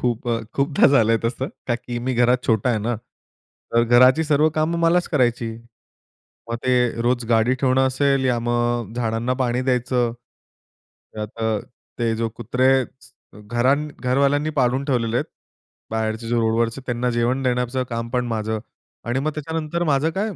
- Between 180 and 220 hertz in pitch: No, low, 125 Hz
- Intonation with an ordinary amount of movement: No, narrow, 2.3 semitones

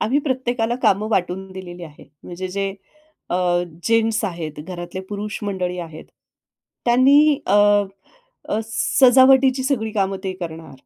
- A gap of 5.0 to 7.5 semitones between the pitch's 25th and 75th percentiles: Yes, wide, 5.5 semitones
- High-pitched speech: Yes, high, 205 Hz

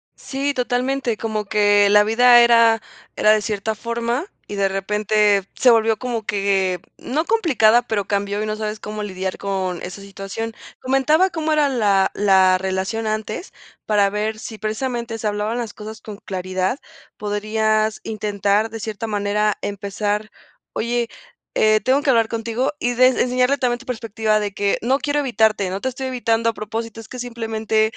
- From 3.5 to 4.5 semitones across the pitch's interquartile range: No, average, 2.7 semitones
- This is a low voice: No, high, 220 Hz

